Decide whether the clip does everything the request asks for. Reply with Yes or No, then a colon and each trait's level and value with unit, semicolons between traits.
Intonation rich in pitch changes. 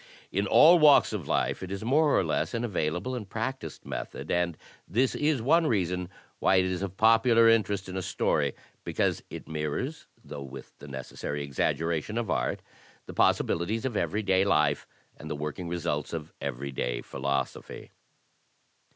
Yes: wide, 6.9 semitones